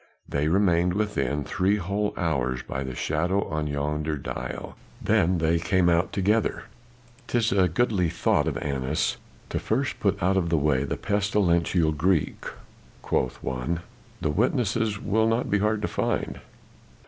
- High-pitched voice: No, very low, 85 Hz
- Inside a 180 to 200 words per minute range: No, average, 150 wpm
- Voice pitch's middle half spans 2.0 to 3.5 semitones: No, average, 5.3 semitones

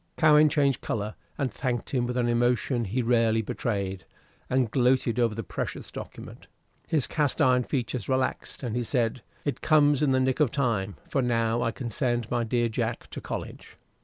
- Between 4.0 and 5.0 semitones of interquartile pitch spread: No, narrow, 2.4 semitones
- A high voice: No, low, 120 Hz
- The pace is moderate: Yes, average, 185 wpm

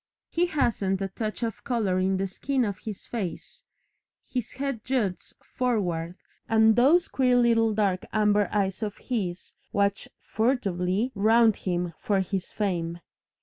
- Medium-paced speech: Yes, average, 145 wpm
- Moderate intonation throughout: Yes, average, 3.9 semitones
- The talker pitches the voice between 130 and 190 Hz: No, high, 210 Hz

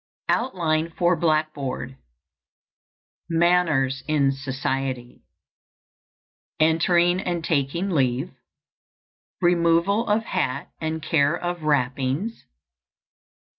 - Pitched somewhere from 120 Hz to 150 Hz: No, medium, 160 Hz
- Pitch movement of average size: Yes, average, 4.3 semitones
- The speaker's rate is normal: No, slow, 75 wpm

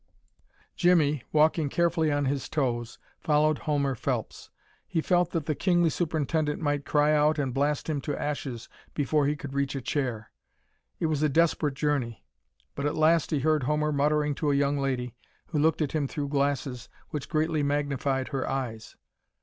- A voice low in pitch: No, medium, 145 Hz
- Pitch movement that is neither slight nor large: No, narrow, 2.0 semitones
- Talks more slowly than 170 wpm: No, average, 175 wpm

